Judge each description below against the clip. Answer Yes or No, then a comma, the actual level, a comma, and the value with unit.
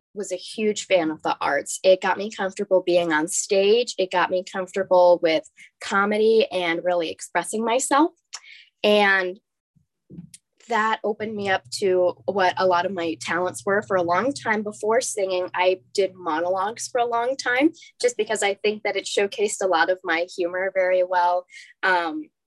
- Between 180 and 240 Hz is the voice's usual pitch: Yes, high, 190 Hz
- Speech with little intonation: No, average, 3.1 semitones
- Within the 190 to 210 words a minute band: No, average, 175 wpm